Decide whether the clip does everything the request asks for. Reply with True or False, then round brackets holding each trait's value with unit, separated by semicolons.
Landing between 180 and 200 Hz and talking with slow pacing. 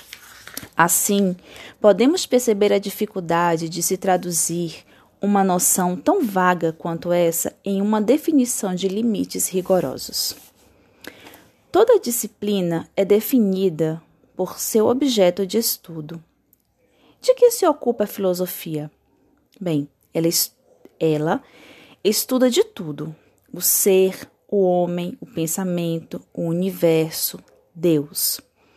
True (185 Hz; 105 wpm)